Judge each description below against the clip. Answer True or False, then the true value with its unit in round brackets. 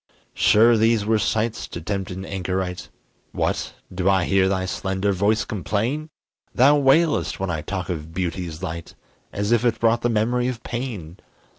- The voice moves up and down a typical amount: True (4.1 semitones)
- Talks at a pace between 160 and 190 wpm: True (165 wpm)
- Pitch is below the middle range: True (100 Hz)